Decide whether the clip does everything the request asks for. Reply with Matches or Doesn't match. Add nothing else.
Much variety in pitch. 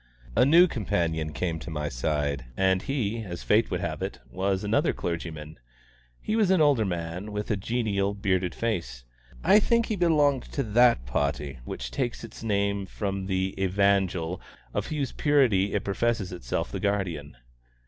Matches